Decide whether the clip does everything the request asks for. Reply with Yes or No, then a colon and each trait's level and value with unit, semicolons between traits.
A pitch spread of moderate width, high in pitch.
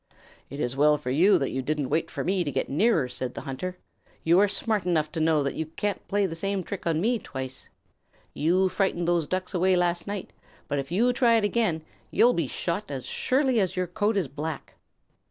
No: average, 5.0 semitones; medium, 175 Hz